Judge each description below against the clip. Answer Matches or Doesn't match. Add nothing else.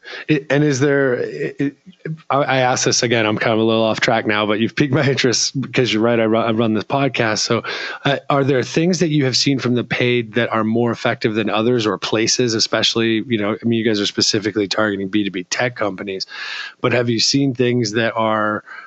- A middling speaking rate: Doesn't match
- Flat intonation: Doesn't match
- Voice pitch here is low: Matches